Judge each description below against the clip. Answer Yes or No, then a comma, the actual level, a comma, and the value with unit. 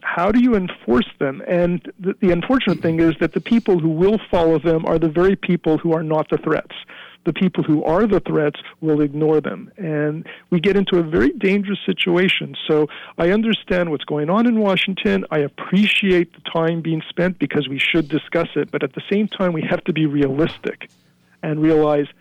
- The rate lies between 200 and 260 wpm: Yes, fast, 205 wpm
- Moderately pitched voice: Yes, medium, 170 Hz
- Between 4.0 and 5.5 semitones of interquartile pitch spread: No, average, 3.5 semitones